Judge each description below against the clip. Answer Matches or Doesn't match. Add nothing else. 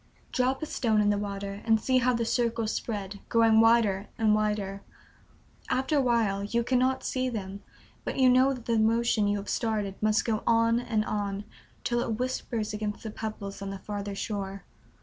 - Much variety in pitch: Doesn't match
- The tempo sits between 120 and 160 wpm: Doesn't match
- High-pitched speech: Matches